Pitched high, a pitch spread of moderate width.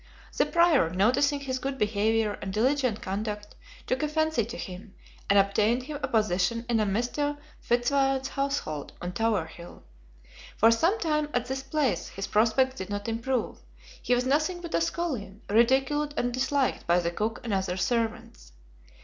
Yes: high, 240 Hz; average, 5.0 semitones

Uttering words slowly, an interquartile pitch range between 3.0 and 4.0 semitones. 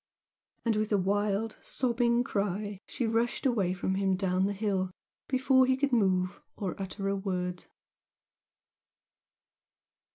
Yes: slow, 130 wpm; average, 3.7 semitones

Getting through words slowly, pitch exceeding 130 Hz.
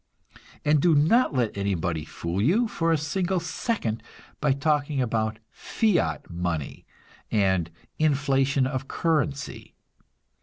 Yes: slow, 120 wpm; medium, 140 Hz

